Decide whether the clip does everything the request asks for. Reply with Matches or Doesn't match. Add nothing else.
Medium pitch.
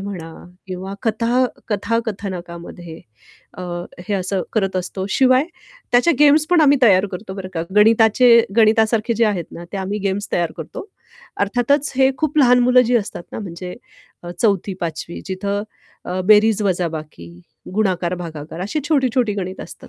Doesn't match